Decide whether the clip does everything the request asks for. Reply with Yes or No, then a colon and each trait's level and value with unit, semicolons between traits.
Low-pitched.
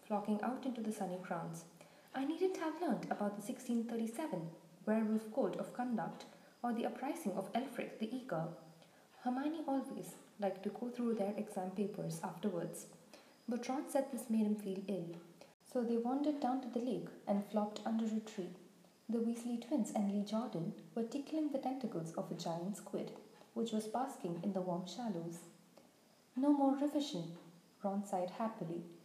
No: high, 215 Hz